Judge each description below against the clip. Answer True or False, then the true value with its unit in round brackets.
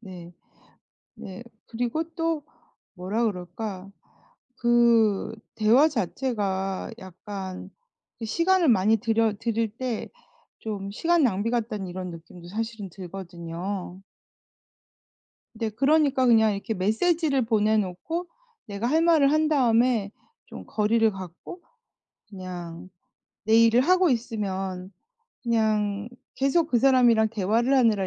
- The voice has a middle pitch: False (220 Hz)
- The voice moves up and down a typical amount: True (4.3 semitones)